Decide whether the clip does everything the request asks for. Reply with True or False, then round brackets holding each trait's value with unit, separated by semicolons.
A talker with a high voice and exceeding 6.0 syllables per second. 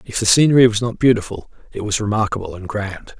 False (110 Hz; 6.3 syllables/s)